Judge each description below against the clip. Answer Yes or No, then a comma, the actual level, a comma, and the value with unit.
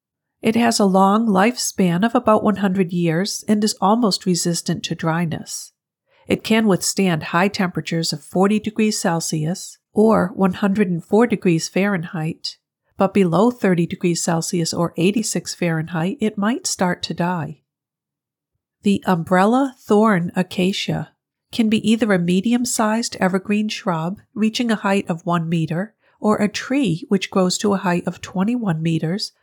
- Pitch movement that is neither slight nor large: Yes, average, 3.7 semitones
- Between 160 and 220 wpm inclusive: No, average, 145 wpm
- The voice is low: No, high, 190 Hz